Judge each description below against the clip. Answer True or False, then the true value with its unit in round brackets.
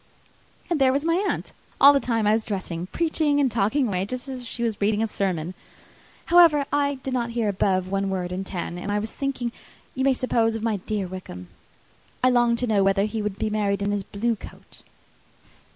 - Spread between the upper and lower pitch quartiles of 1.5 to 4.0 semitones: False (4.6 semitones)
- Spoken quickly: True (215 wpm)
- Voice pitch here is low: False (220 Hz)